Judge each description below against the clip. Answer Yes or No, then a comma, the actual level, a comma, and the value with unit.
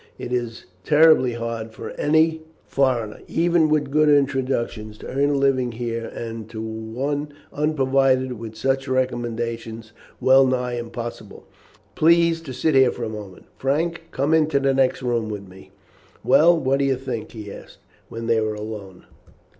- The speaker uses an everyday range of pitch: Yes, average, 3.7 semitones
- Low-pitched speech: Yes, low, 130 Hz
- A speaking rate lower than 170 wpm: Yes, average, 160 wpm